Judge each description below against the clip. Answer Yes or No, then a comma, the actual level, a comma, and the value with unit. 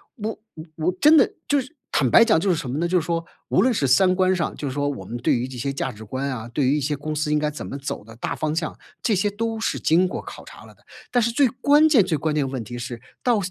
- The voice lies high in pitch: No, medium, 155 Hz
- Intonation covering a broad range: Yes, wide, 7.3 semitones